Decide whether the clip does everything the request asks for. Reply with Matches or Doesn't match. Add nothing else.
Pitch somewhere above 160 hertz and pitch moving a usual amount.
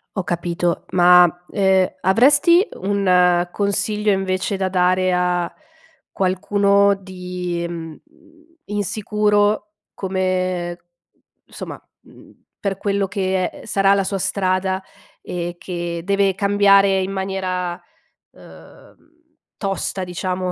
Doesn't match